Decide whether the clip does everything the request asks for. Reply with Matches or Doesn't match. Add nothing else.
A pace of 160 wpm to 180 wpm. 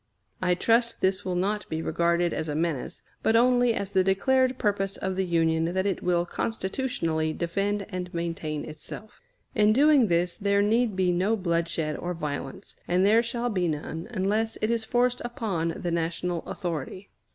Matches